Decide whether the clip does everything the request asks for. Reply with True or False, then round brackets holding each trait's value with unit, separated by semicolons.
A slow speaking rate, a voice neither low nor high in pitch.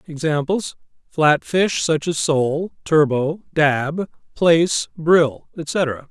True (100 wpm; 155 Hz)